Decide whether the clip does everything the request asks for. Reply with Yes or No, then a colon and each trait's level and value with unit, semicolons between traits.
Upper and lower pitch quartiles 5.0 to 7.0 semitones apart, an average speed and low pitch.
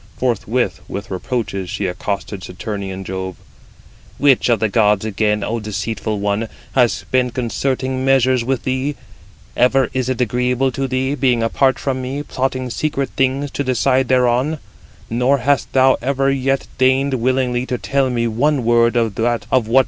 No: average, 2.8 semitones; average, 165 wpm; low, 125 Hz